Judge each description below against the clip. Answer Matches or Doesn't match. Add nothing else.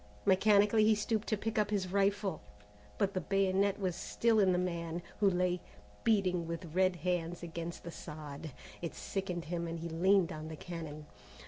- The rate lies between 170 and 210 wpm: Matches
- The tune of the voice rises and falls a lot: Doesn't match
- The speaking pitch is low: Doesn't match